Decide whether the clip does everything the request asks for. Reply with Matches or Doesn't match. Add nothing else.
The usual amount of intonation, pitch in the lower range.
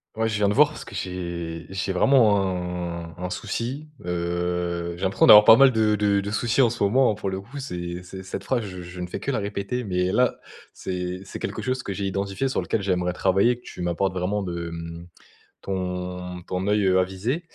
Matches